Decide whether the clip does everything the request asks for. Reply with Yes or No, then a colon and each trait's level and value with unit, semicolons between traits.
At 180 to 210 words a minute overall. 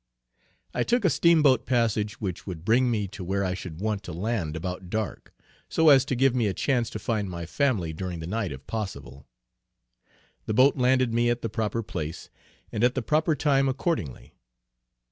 Yes: average, 190 wpm